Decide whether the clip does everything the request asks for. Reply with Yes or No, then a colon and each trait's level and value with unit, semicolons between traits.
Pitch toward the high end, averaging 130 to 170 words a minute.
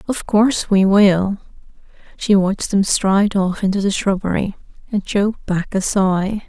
Yes: high, 200 Hz; average, 155 wpm